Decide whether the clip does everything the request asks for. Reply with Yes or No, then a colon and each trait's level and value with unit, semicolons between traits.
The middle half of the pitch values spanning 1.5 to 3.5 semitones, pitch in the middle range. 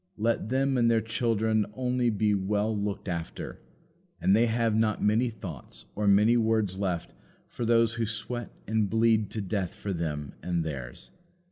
No: average, 2.7 semitones; low, 110 Hz